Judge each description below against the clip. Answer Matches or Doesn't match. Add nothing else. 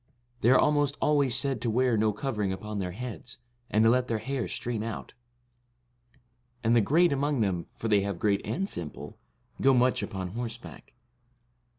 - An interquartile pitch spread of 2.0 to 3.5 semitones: Doesn't match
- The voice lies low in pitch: Matches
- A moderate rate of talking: Matches